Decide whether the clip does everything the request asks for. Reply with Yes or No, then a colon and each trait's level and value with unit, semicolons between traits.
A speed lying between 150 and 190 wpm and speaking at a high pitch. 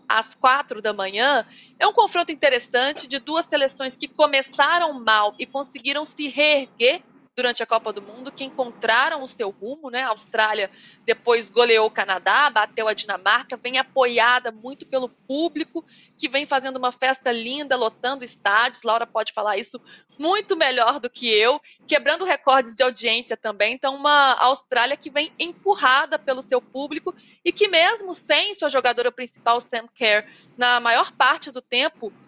Yes: average, 165 wpm; very high, 255 Hz